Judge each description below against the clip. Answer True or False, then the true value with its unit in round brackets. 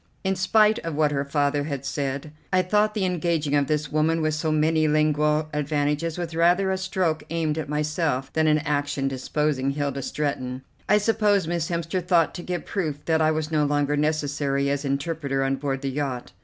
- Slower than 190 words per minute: False (195 wpm)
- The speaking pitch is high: False (150 Hz)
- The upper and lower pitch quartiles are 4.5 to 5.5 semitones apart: False (2.7 semitones)